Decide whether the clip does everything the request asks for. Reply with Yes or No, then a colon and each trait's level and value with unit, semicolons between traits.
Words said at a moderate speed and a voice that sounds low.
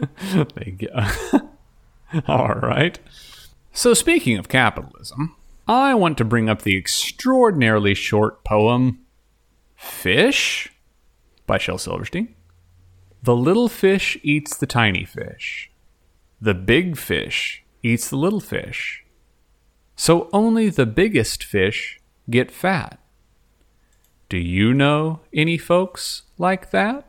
No: slow, 115 wpm; low, 120 Hz